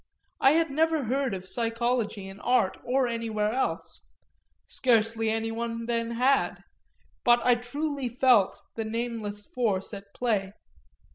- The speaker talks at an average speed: No, slow, 130 wpm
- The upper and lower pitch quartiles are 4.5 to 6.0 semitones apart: No, narrow, 2.5 semitones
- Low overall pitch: No, high, 230 Hz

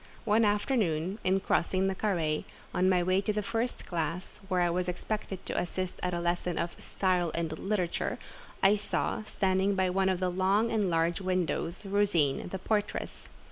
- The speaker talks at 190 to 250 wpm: No, average, 180 wpm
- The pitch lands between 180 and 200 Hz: Yes, medium, 185 Hz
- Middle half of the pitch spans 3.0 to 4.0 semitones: No, narrow, 2.4 semitones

